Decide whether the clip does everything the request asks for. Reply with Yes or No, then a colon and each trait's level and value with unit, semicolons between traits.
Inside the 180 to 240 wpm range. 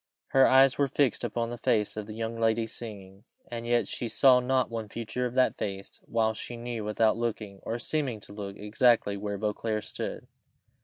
Yes: average, 195 wpm